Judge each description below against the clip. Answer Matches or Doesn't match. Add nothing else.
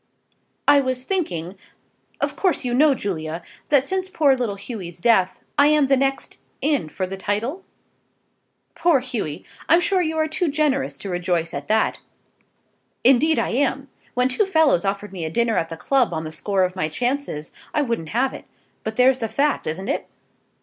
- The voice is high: Matches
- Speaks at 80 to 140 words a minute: Doesn't match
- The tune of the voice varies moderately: Doesn't match